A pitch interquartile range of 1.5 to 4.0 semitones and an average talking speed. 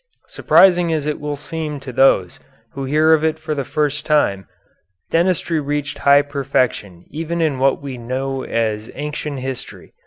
Yes: average, 2.7 semitones; average, 160 wpm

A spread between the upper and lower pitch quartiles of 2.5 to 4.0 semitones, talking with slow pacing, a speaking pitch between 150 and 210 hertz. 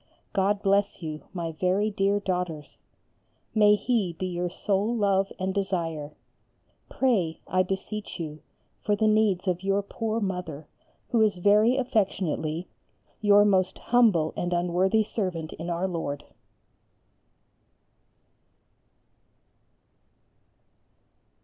Yes: average, 3.1 semitones; slow, 110 wpm; high, 190 Hz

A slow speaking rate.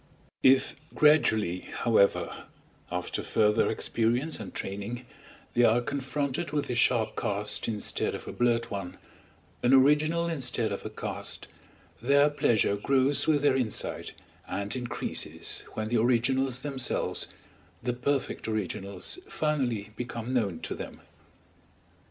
Yes: slow, 125 wpm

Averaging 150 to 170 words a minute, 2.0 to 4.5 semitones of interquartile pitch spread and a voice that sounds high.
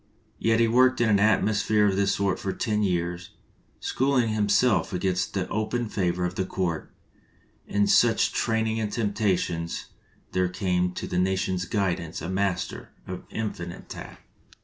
No: average, 165 wpm; average, 3.3 semitones; low, 100 Hz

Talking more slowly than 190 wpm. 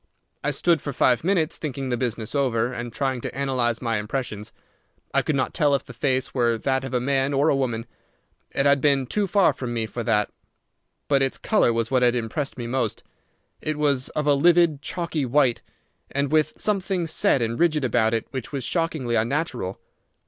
No: average, 200 wpm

